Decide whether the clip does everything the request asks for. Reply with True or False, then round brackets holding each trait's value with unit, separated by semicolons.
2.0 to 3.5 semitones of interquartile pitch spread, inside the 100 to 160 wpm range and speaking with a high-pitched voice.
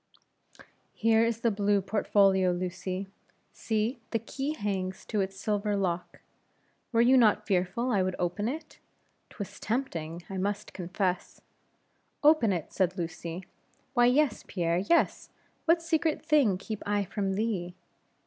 False (3.9 semitones; 140 wpm; 205 Hz)